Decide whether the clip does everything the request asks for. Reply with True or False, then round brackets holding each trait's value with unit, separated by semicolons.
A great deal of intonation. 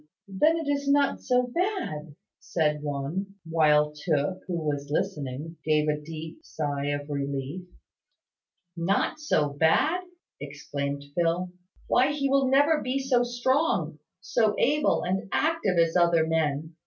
True (9.0 semitones)